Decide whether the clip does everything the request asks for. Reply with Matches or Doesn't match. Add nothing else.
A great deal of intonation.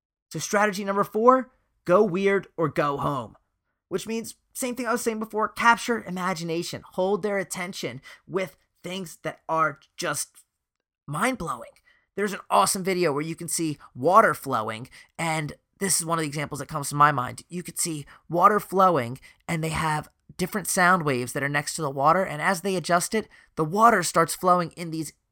Doesn't match